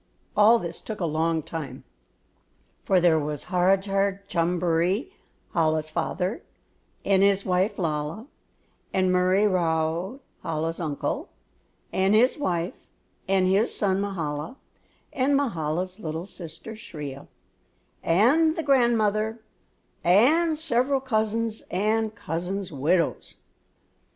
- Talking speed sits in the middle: No, slow, 105 wpm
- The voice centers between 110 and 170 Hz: No, high, 190 Hz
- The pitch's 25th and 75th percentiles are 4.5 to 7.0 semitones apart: Yes, average, 4.8 semitones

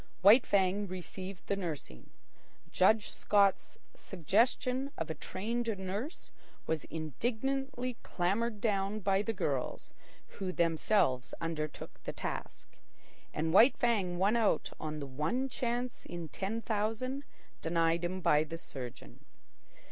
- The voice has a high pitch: Yes, high, 195 Hz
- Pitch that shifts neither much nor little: No, wide, 5.7 semitones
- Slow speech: Yes, slow, 125 wpm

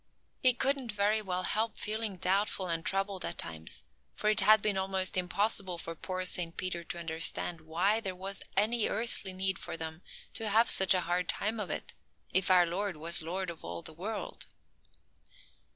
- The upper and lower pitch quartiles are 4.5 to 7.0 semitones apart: No, average, 3.4 semitones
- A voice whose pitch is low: No, high, 190 Hz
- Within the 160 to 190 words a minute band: Yes, average, 185 wpm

